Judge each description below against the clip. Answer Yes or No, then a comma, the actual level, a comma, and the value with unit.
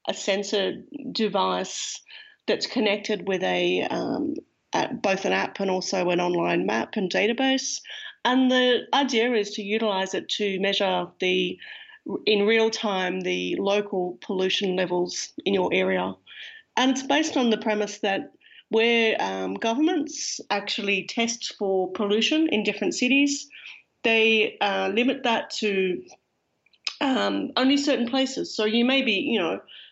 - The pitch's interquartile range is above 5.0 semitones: Yes, wide, 5.5 semitones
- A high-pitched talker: Yes, high, 220 Hz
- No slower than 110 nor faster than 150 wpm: Yes, average, 140 wpm